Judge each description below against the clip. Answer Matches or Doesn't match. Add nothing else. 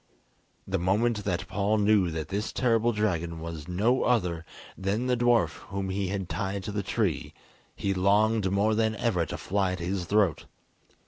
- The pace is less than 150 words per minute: Doesn't match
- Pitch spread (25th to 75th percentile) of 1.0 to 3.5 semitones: Matches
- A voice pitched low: Matches